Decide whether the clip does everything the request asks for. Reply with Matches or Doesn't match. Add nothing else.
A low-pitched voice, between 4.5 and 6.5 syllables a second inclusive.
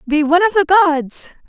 Doesn't match